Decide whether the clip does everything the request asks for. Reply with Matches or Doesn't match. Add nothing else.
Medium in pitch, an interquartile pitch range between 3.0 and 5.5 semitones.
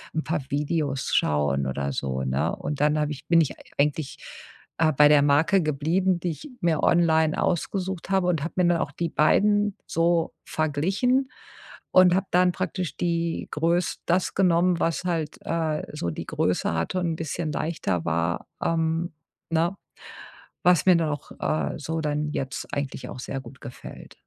Matches